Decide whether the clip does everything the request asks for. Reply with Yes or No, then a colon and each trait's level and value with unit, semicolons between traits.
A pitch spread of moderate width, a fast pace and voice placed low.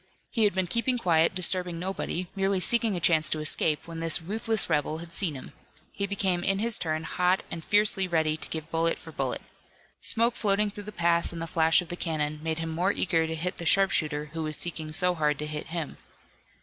No: average, 3.3 semitones; fast, 220 wpm; medium, 170 Hz